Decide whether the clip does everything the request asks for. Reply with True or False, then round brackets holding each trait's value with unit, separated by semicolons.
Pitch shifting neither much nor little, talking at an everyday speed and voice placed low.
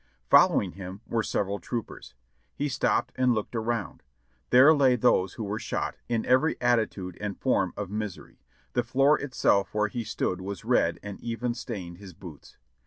True (3.8 semitones; 170 wpm; 110 Hz)